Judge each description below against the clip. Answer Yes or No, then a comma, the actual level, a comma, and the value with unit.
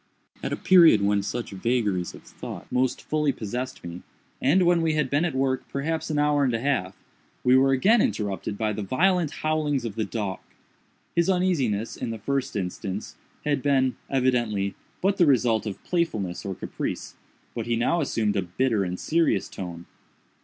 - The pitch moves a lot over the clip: Yes, wide, 6.4 semitones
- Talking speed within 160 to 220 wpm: Yes, average, 180 wpm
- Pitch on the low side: Yes, low, 125 Hz